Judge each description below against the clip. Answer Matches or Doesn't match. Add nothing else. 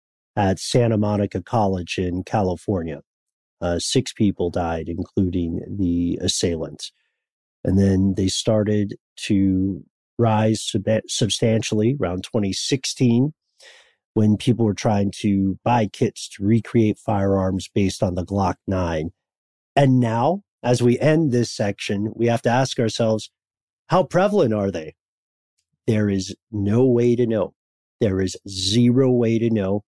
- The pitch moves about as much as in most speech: Matches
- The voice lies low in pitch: Matches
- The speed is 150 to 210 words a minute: Doesn't match